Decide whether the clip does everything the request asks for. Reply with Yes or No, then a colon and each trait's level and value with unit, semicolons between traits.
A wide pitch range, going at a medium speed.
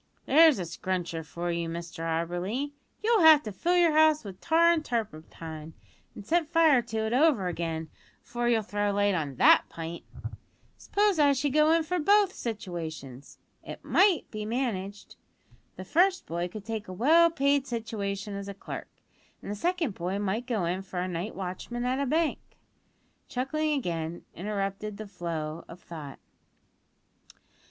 Yes: wide, 8.9 semitones; average, 160 wpm